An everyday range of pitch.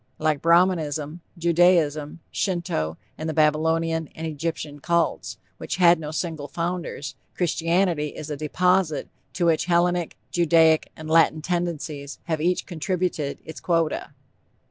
No: narrow, 2.1 semitones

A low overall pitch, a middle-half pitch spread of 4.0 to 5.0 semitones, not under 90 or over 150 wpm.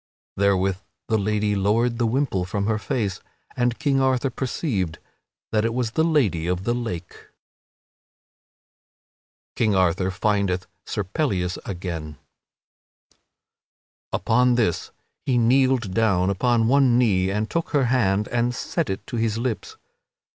Yes: low, 110 Hz; average, 4.4 semitones; slow, 135 wpm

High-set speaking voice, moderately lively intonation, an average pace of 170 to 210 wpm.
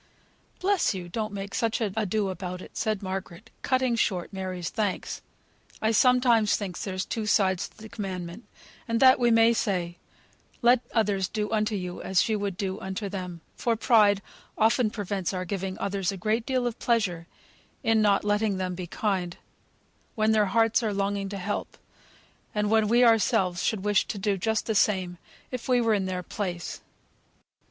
Yes: high, 205 Hz; average, 3.1 semitones; average, 175 wpm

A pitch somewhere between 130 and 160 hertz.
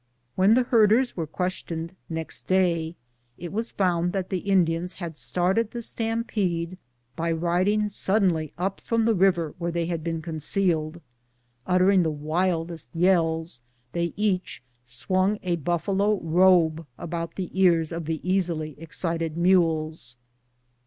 No: medium, 175 Hz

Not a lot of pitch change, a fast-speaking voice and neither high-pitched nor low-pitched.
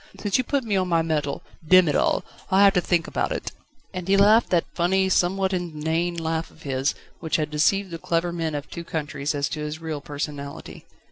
No: average, 3.7 semitones; fast, 215 wpm; medium, 165 Hz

